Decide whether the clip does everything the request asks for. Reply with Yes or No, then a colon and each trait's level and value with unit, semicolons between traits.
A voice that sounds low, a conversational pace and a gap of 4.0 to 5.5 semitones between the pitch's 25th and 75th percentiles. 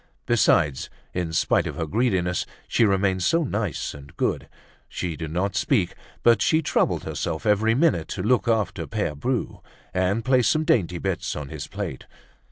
Yes: low, 100 Hz; average, 170 wpm; average, 5.2 semitones